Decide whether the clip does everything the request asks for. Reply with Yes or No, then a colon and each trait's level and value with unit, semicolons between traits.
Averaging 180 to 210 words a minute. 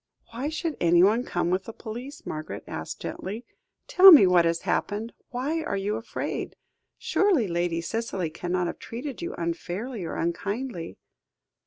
No: average, 150 wpm